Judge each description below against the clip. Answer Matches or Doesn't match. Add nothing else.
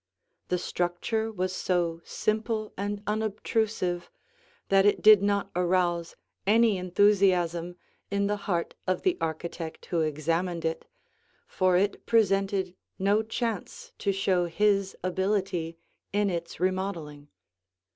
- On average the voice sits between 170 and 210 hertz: Matches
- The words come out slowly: Matches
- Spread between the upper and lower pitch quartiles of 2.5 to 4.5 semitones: Matches